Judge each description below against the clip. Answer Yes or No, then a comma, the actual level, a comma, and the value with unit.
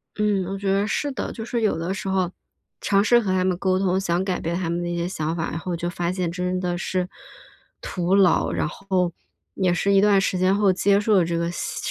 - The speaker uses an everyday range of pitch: No, narrow, 2.2 semitones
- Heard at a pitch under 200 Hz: Yes, medium, 185 Hz